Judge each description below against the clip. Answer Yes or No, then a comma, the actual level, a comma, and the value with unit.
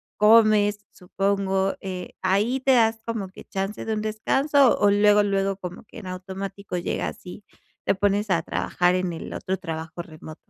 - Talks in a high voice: Yes, high, 195 Hz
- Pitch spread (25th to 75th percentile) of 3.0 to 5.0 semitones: No, narrow, 2.5 semitones